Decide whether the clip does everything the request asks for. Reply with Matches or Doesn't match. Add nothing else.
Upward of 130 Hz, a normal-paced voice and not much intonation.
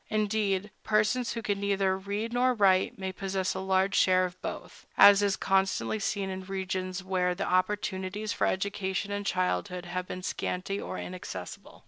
Matches